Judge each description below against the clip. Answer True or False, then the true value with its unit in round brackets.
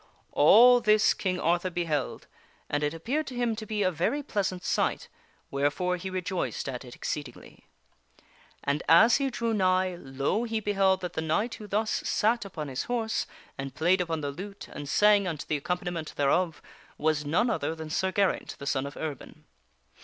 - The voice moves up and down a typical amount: False (5.7 semitones)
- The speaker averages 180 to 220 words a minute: True (185 wpm)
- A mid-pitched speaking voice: True (180 Hz)